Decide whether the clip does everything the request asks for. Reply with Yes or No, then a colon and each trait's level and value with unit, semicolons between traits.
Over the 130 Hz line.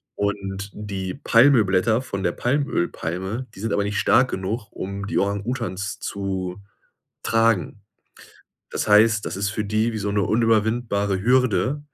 No: low, 105 Hz